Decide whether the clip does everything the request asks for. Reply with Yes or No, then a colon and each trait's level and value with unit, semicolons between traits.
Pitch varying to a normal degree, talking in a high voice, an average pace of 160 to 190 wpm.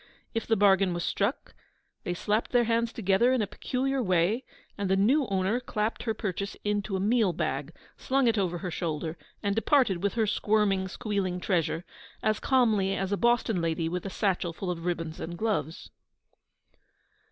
Yes: average, 3.9 semitones; high, 200 Hz; average, 175 wpm